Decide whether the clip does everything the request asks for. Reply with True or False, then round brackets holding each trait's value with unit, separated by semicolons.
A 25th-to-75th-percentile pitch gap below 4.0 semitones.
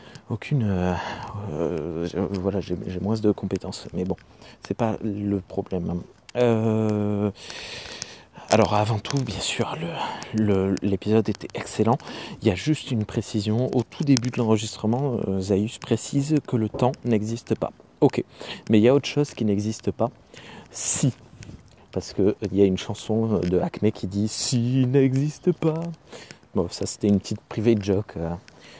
True (3.4 semitones)